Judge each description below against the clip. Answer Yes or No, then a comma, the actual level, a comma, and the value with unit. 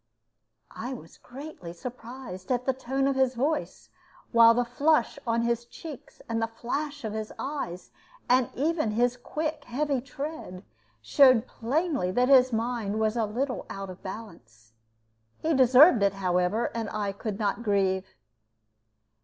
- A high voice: Yes, high, 240 Hz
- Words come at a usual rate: Yes, average, 150 wpm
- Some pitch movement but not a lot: Yes, average, 4.2 semitones